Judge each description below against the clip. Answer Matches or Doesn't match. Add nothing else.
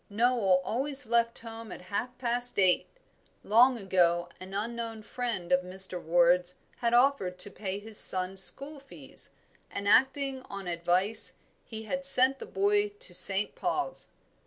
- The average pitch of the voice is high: Matches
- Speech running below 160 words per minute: Matches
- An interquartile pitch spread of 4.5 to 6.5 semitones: Matches